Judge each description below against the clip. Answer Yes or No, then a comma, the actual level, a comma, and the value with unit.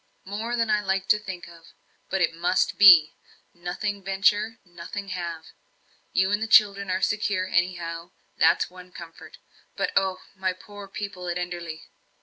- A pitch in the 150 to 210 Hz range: Yes, medium, 185 Hz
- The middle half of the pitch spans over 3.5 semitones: No, average, 2.7 semitones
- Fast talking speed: No, average, 155 wpm